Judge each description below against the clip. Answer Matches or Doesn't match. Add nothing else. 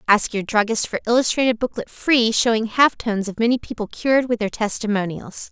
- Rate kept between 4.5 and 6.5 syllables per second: Matches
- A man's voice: Doesn't match